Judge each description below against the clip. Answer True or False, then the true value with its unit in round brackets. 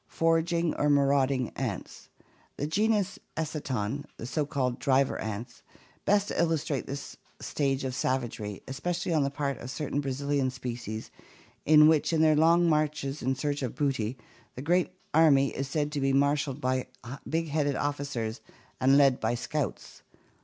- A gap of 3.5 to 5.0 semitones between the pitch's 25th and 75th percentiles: False (2.8 semitones)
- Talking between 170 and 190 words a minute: False (155 wpm)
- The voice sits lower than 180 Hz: True (140 Hz)